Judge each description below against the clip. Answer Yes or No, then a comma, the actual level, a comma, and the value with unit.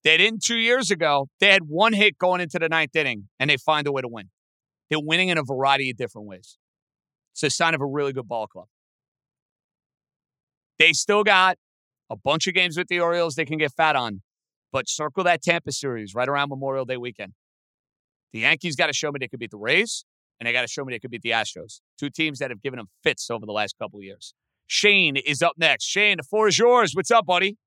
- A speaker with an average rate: No, fast, 240 wpm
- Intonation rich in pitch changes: Yes, wide, 6.1 semitones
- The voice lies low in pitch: No, medium, 150 Hz